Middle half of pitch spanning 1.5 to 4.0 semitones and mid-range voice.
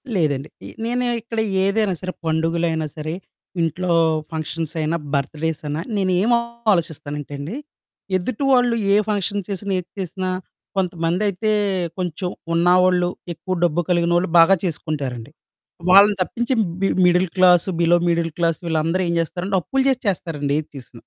Yes: average, 3.3 semitones; medium, 175 Hz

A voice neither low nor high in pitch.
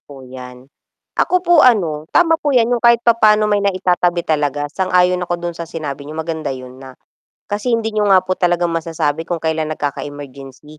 Yes: medium, 170 Hz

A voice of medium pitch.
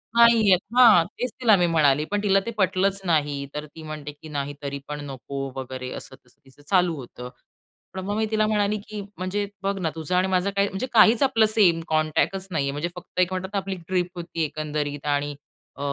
Yes: medium, 180 Hz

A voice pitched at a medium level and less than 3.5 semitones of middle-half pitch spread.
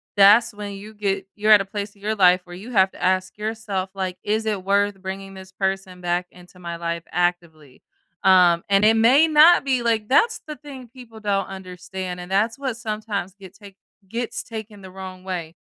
No: high, 195 Hz; average, 2.8 semitones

